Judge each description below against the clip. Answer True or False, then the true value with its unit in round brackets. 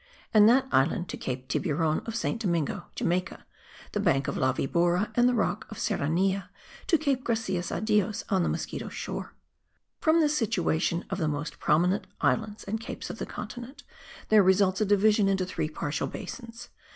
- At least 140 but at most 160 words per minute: False (175 wpm)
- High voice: True (195 Hz)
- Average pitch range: True (4.6 semitones)